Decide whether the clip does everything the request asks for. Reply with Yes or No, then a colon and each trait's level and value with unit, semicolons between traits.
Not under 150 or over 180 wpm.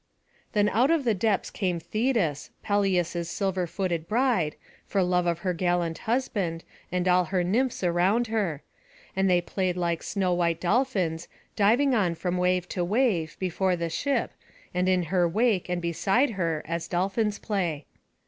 Yes: average, 160 wpm